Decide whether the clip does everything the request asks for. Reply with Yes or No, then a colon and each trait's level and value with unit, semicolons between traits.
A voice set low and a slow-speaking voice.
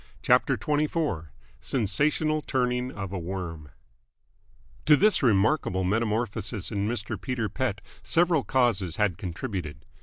Yes: low, 110 Hz; slow, 115 wpm